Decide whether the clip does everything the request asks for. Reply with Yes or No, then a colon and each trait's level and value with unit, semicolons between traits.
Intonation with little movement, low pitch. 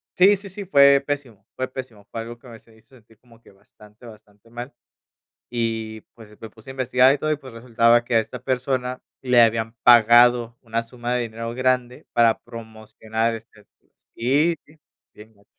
Yes: narrow, 2.3 semitones; low, 120 Hz